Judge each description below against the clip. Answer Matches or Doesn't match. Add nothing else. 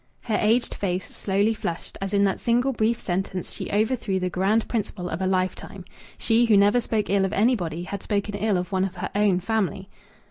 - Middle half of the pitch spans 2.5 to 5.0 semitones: Matches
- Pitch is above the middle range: Matches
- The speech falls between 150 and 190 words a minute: Doesn't match